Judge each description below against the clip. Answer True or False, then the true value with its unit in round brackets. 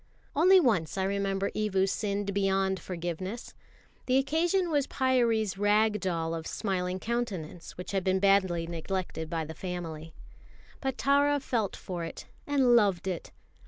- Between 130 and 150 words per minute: True (145 wpm)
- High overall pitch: True (195 Hz)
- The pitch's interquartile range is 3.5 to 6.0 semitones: True (5.0 semitones)